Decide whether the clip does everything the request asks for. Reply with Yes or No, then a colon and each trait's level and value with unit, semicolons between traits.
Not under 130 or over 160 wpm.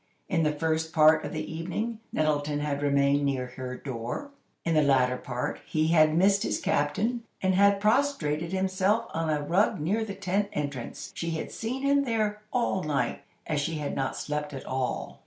No: average, 185 wpm